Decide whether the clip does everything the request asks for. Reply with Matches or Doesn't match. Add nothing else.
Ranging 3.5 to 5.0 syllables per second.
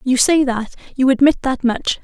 Matches